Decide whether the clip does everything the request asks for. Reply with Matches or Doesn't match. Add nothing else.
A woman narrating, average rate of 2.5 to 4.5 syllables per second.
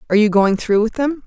Doesn't match